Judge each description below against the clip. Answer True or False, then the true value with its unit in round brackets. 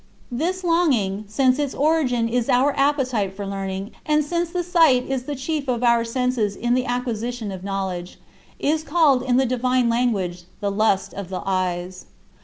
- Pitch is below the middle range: False (245 Hz)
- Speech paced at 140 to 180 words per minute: True (175 wpm)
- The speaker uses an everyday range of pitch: False (5.7 semitones)